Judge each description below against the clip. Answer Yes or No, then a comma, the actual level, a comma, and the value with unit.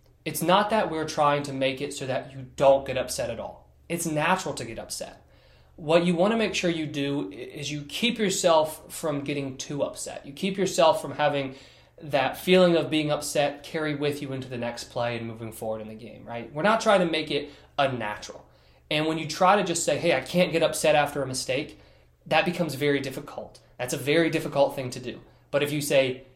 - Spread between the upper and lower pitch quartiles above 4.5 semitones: No, average, 3.6 semitones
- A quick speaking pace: Yes, fast, 225 wpm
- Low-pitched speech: No, medium, 145 Hz